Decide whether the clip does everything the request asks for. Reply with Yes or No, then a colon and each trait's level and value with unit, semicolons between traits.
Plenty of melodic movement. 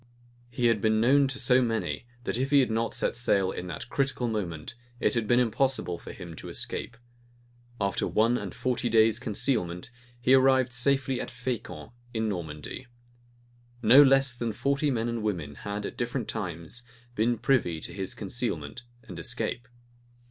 No: average, 3.8 semitones